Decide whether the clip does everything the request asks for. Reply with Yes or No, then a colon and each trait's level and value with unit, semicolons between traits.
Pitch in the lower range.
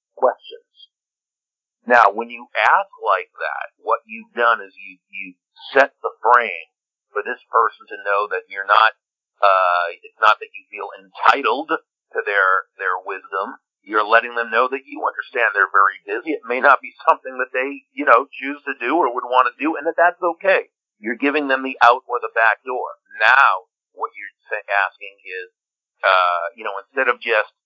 No: medium, 150 Hz